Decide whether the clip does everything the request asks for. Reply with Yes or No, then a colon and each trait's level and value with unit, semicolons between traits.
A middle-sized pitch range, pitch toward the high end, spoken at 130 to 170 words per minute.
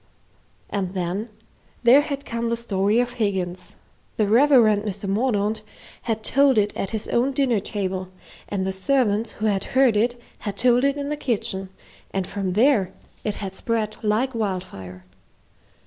Yes: average, 3.9 semitones; high, 215 Hz; average, 160 wpm